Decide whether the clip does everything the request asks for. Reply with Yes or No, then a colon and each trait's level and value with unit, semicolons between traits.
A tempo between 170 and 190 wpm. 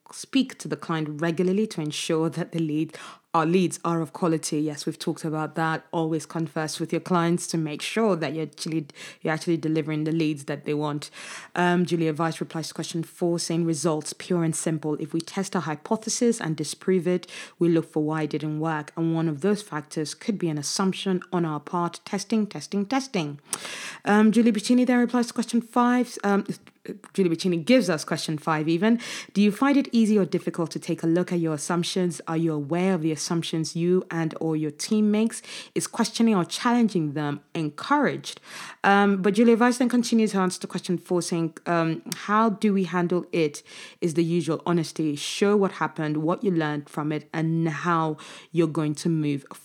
No: average, 200 wpm